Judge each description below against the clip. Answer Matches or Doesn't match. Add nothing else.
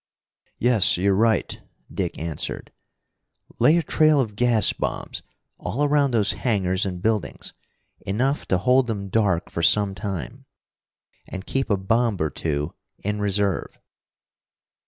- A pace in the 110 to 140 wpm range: Matches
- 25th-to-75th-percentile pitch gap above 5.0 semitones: Doesn't match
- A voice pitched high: Doesn't match